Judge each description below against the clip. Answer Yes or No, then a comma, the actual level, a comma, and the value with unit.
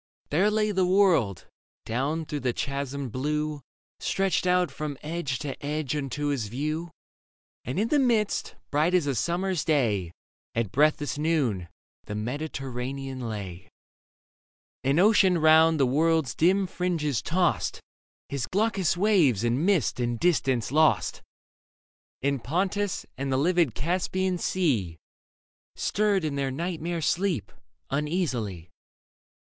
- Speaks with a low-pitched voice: No, medium, 150 Hz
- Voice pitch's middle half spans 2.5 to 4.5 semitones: No, average, 5.3 semitones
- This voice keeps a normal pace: No, slow, 125 wpm